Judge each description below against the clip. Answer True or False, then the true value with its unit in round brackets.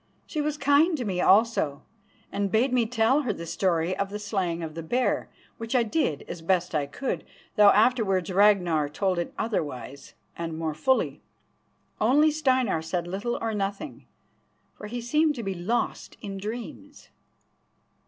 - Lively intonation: True (6.0 semitones)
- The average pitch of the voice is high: True (205 Hz)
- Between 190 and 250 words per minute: False (165 wpm)